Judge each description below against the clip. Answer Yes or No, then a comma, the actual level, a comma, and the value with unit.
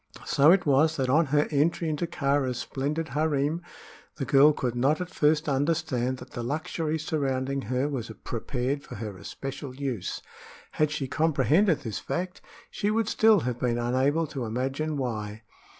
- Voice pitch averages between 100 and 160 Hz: Yes, medium, 140 Hz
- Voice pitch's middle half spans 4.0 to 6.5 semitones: No, average, 3.5 semitones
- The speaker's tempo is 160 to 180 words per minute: Yes, average, 165 wpm